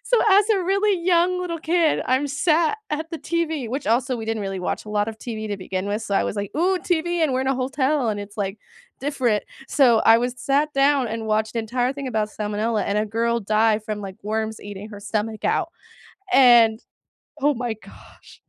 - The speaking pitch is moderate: No, high, 235 Hz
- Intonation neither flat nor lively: No, wide, 5.8 semitones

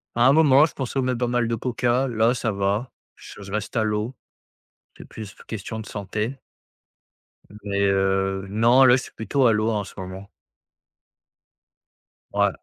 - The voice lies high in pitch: No, low, 110 Hz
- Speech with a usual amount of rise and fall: Yes, average, 3.6 semitones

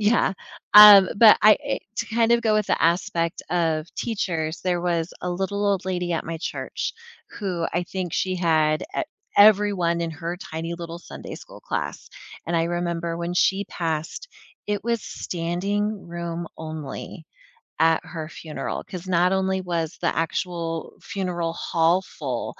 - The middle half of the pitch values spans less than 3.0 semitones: Yes, narrow, 2.6 semitones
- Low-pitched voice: No, medium, 175 Hz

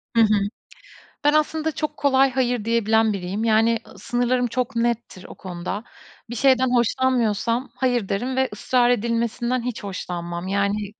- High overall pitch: Yes, high, 235 Hz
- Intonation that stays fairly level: No, average, 3.4 semitones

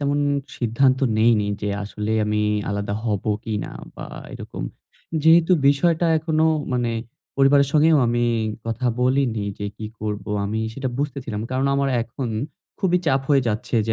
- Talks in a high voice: No, low, 125 Hz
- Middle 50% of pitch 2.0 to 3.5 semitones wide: No, average, 4.5 semitones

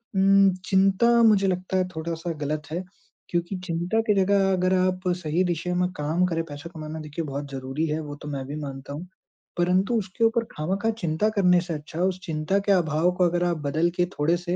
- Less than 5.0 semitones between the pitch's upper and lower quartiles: Yes, average, 3.5 semitones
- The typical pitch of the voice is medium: Yes, medium, 175 Hz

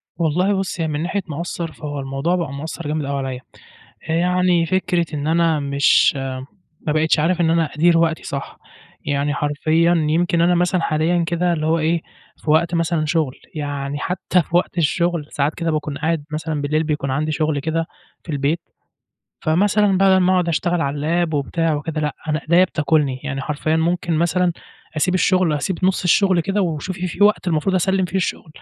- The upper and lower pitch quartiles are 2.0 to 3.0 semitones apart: Yes, average, 2.7 semitones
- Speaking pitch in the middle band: Yes, medium, 165 Hz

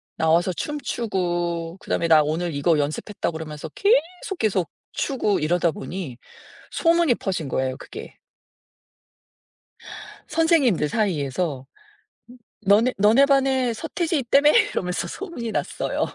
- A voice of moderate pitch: No, high, 195 Hz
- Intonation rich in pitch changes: Yes, wide, 8.9 semitones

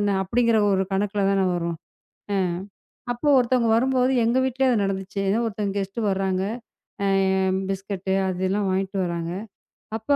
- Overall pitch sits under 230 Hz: Yes, high, 195 Hz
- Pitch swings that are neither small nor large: Yes, average, 3.5 semitones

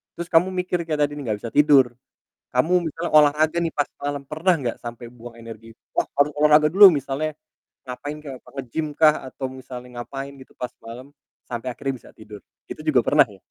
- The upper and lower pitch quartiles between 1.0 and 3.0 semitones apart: No, average, 3.8 semitones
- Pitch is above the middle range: No, medium, 140 Hz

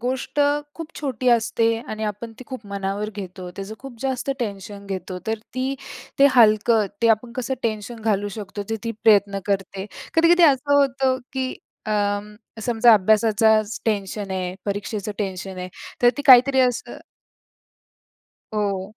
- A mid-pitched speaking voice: No, high, 215 Hz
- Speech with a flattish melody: No, average, 3.8 semitones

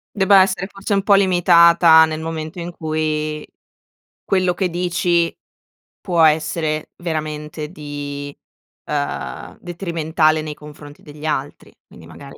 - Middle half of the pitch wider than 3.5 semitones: No, narrow, 2.5 semitones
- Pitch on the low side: No, medium, 160 Hz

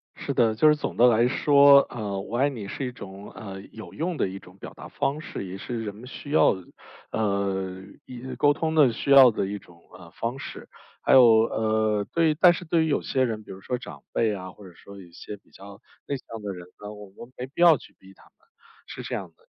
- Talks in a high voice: No, low, 110 Hz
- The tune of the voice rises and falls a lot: Yes, wide, 5.8 semitones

